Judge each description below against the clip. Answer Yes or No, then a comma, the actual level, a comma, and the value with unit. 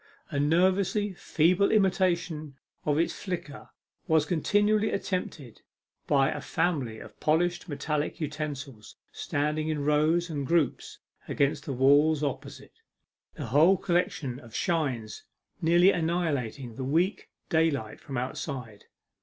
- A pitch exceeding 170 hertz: No, medium, 155 Hz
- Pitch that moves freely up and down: No, average, 3.8 semitones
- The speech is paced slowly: Yes, slow, 120 wpm